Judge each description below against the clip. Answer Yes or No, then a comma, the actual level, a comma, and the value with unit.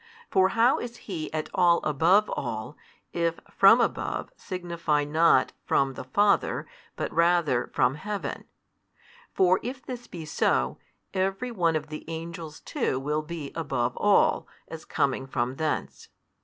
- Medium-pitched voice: Yes, medium, 165 Hz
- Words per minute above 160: No, average, 145 wpm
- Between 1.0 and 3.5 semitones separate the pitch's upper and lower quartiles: No, average, 4.4 semitones